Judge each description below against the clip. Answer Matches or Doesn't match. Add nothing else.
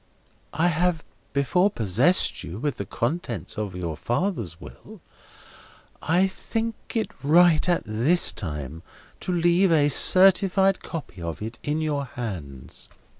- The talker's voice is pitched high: Doesn't match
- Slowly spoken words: Matches